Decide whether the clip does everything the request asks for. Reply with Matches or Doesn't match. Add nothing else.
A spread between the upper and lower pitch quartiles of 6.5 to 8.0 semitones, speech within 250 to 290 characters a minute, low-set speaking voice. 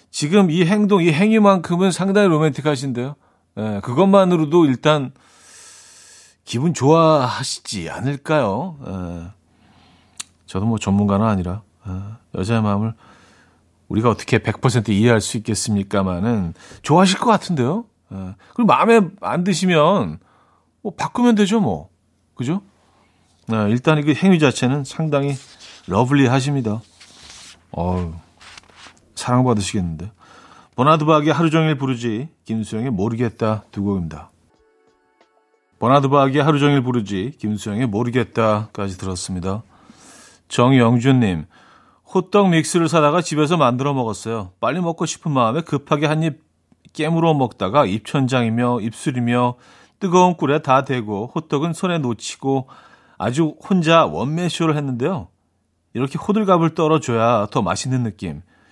Matches